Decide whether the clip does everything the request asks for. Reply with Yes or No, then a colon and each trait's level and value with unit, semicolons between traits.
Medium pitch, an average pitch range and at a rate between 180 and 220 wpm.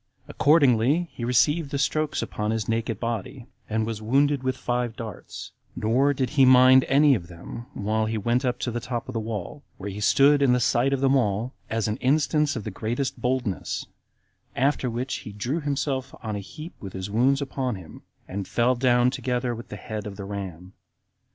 No: low, 120 Hz; average, 3.8 semitones; average, 200 wpm